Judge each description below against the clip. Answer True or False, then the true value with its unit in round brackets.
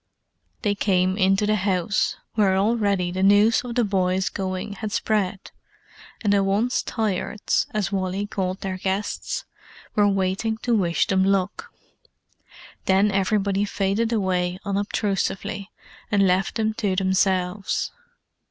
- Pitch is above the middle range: True (195 Hz)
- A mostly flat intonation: True (1.9 semitones)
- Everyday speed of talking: False (130 wpm)